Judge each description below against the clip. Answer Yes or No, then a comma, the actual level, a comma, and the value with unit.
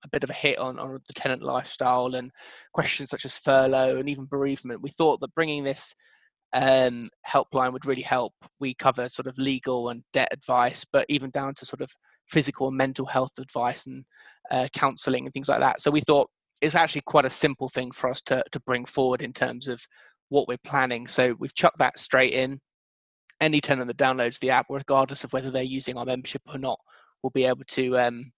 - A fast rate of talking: Yes, fast, 215 wpm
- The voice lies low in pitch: Yes, low, 130 Hz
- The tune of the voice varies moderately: No, narrow, 1.7 semitones